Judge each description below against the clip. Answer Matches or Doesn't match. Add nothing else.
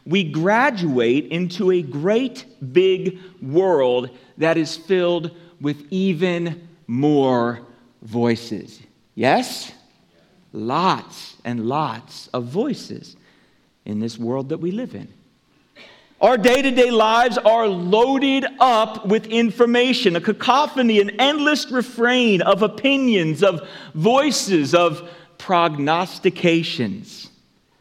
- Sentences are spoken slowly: Matches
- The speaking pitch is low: Doesn't match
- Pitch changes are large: Matches